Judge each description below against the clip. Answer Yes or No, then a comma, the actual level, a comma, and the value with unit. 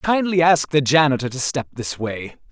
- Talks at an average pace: Yes, average, 190 wpm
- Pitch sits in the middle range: Yes, medium, 145 Hz